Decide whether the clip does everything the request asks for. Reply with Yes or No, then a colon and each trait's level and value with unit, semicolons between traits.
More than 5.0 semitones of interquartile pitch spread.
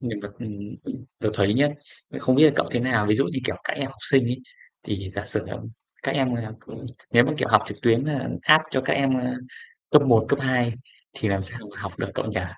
No: average, 3.8 semitones